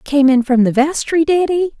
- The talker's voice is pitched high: Yes, very high, 290 Hz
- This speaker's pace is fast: Yes, fast, 235 wpm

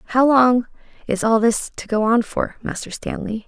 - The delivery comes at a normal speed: Yes, average, 190 wpm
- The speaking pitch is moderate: No, high, 230 Hz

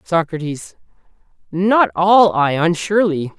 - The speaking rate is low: Yes, slow, 90 wpm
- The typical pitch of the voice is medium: Yes, medium, 180 Hz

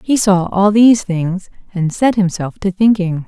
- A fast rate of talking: No, average, 185 wpm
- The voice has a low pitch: No, high, 195 Hz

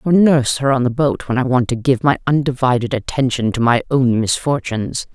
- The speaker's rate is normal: No, fast, 210 wpm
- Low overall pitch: Yes, low, 130 Hz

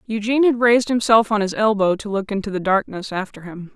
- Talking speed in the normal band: No, fast, 225 wpm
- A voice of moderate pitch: No, high, 210 Hz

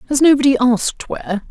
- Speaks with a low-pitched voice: No, very high, 260 Hz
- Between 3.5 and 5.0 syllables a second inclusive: No, 6.5 syllables/s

